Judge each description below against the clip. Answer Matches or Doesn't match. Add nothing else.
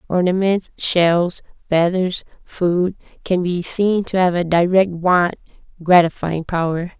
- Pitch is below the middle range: Doesn't match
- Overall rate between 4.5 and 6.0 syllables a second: Doesn't match